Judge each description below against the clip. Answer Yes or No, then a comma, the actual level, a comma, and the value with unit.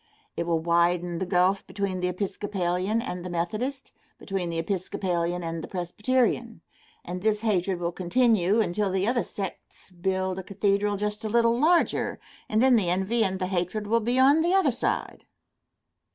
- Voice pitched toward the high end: Yes, high, 195 Hz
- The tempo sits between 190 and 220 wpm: No, average, 170 wpm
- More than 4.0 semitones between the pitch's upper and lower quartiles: No, average, 3.7 semitones